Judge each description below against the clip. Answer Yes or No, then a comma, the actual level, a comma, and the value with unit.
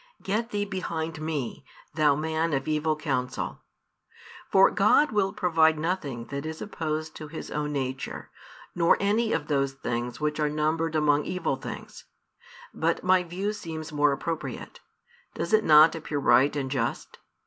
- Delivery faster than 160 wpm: No, average, 155 wpm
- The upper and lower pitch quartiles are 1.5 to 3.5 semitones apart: Yes, average, 2.7 semitones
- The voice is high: No, medium, 155 Hz